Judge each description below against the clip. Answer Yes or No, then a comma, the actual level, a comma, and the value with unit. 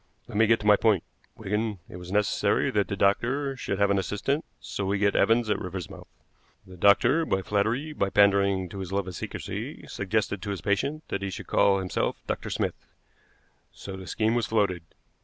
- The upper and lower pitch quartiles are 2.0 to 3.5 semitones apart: Yes, narrow, 2.4 semitones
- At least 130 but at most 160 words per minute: No, average, 195 wpm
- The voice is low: Yes, low, 100 Hz